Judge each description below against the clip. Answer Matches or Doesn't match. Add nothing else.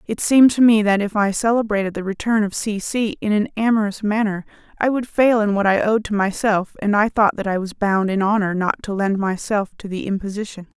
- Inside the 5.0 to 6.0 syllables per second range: Matches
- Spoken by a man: Doesn't match